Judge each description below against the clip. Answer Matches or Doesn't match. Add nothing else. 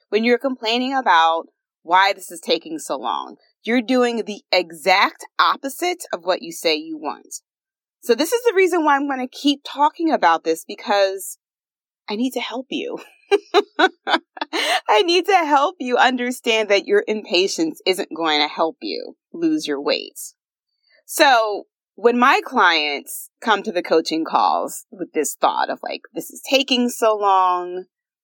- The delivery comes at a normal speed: Matches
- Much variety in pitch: Matches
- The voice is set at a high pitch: Matches